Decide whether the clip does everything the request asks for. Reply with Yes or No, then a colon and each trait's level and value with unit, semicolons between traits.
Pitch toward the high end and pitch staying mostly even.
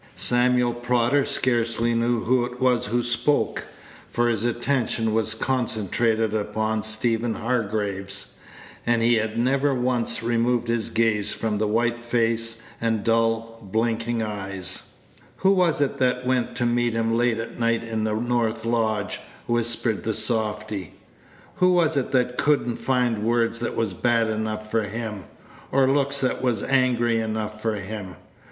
No: low, 115 Hz; narrow, 1.8 semitones